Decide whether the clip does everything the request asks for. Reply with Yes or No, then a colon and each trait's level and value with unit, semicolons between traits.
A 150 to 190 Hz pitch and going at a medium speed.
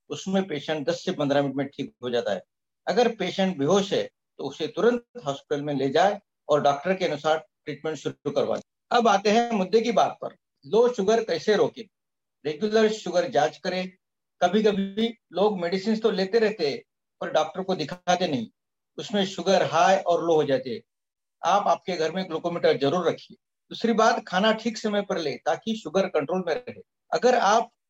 Yes: medium, 185 Hz; average, 180 wpm